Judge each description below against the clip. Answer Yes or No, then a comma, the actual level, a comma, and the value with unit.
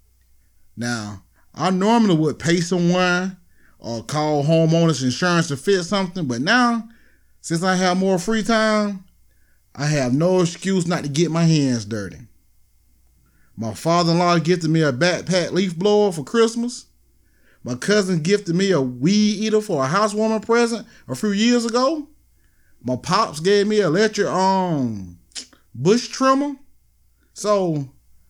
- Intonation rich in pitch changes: Yes, wide, 8.3 semitones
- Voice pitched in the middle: Yes, medium, 175 Hz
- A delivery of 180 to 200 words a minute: No, average, 140 wpm